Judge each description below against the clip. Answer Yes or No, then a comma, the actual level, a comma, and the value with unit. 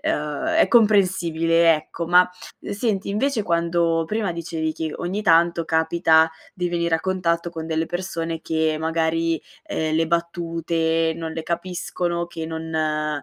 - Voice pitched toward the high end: No, medium, 165 Hz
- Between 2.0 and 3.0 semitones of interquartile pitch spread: No, narrow, 1.4 semitones